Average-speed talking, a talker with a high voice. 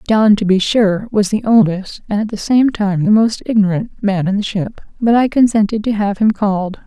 No: fast, 225 wpm; high, 210 Hz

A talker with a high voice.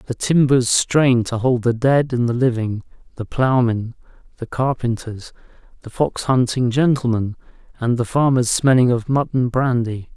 No: low, 125 Hz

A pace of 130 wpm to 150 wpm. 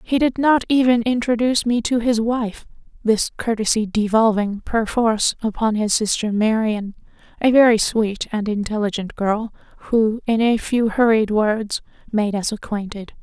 Yes: average, 140 wpm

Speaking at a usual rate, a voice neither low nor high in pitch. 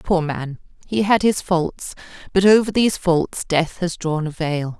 Yes: average, 190 wpm; medium, 175 Hz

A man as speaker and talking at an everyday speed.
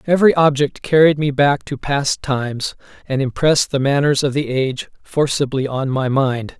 Yes: male; average, 175 wpm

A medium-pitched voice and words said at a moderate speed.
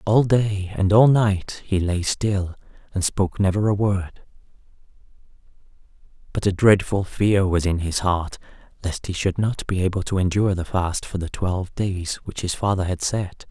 No: very low, 95 Hz; average, 180 wpm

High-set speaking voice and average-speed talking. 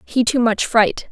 No: high, 235 Hz; fast, 215 wpm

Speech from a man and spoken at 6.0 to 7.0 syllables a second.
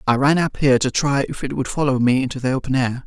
Yes: male; 6.5 syllables/s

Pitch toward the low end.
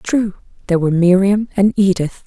No: high, 190 Hz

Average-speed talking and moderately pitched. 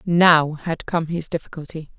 Yes: average, 150 wpm; medium, 160 Hz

